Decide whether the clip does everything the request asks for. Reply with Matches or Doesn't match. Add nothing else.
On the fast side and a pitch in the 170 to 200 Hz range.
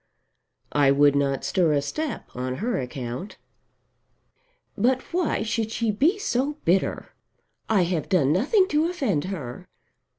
Doesn't match